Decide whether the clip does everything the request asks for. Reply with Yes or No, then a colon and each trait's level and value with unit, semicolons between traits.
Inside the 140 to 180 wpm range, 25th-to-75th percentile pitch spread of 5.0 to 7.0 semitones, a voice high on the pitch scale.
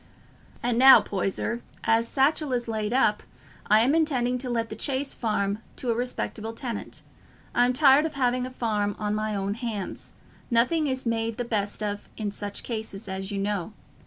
No: average, 175 wpm; average, 3.3 semitones; high, 230 Hz